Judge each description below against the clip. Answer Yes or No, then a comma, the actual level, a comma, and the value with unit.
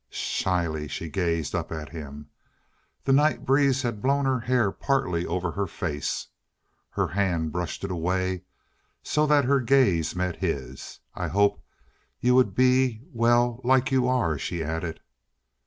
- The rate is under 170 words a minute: Yes, average, 150 wpm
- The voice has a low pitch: Yes, very low, 95 Hz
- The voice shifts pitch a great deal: Yes, wide, 7.4 semitones